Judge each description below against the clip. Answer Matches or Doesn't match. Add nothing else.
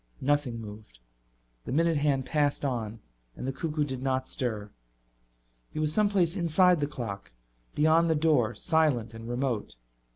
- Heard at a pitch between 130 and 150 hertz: Matches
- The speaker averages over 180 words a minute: Doesn't match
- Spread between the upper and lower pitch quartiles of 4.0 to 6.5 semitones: Matches